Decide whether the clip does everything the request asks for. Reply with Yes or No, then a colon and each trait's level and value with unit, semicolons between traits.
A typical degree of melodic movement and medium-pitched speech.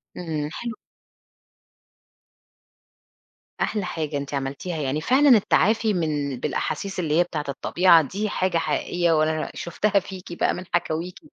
Yes: average, 3.6 semitones; medium, 170 Hz